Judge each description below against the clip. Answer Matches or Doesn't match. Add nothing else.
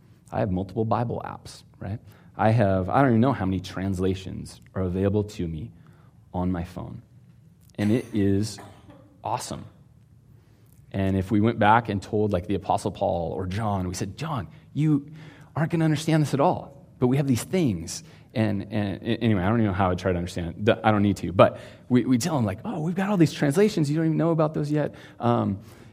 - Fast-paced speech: Matches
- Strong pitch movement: Matches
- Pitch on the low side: Matches